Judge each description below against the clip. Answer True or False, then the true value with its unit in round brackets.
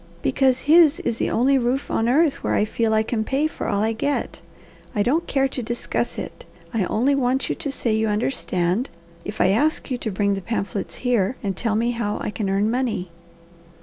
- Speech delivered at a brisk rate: True (215 wpm)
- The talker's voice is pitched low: False (235 Hz)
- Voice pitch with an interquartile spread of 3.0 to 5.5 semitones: True (4.2 semitones)